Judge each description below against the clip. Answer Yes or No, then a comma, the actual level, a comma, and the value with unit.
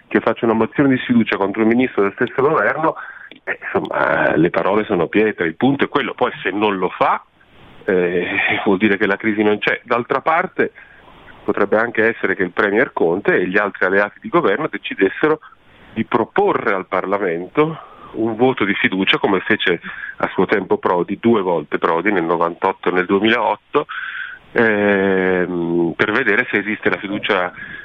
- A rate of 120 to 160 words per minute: No, fast, 170 wpm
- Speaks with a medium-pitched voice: No, low, 105 Hz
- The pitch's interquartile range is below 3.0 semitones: No, average, 3.5 semitones